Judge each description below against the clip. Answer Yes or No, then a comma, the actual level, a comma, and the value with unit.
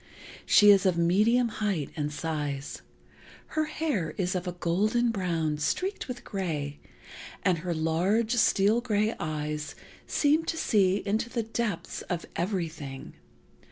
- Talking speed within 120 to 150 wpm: Yes, slow, 135 wpm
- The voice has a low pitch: No, medium, 185 Hz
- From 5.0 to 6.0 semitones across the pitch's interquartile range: Yes, wide, 5.5 semitones